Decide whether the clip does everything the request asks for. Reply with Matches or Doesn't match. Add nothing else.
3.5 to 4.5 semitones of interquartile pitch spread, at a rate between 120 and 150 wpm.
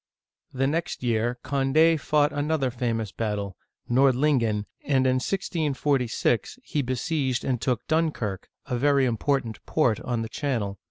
Matches